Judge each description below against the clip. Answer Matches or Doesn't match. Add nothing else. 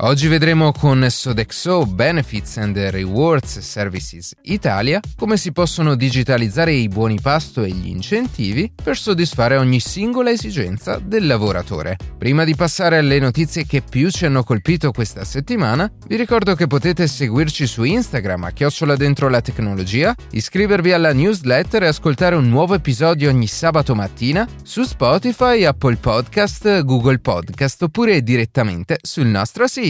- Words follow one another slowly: Doesn't match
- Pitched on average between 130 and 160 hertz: Matches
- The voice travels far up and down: Matches